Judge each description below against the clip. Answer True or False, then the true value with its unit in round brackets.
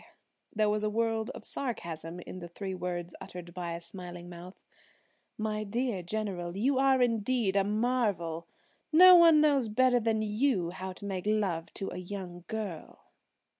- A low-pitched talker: False (205 Hz)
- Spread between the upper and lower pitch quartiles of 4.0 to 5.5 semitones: True (4.5 semitones)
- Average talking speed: True (165 wpm)